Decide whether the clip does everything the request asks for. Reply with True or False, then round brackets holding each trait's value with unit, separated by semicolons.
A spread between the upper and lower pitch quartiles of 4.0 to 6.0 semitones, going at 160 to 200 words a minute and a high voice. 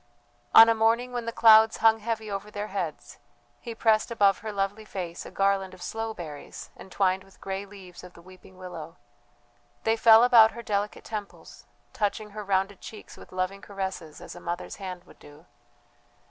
False (3.0 semitones; 180 wpm; 200 Hz)